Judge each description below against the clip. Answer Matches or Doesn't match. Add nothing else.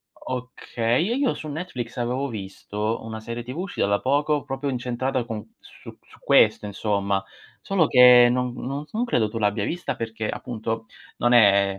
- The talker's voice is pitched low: Matches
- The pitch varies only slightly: Doesn't match